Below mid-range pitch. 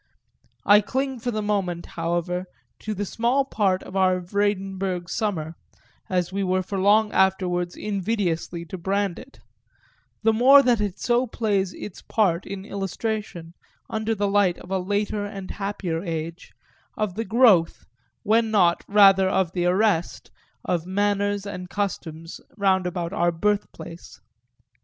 No: high, 195 Hz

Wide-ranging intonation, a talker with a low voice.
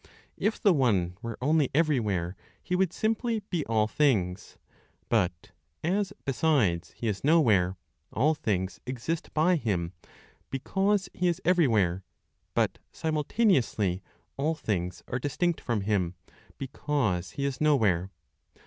Yes: wide, 8.8 semitones; low, 130 Hz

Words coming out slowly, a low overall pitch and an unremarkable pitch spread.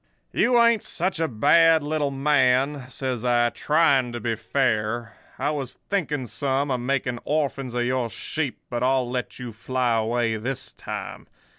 No: average, 160 wpm; low, 130 Hz; average, 3.3 semitones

